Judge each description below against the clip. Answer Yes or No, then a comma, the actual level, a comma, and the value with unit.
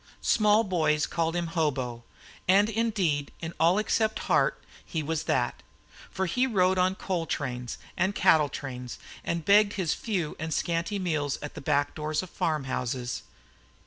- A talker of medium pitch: Yes, medium, 165 Hz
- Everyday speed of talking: Yes, average, 160 wpm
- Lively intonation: No, average, 4.6 semitones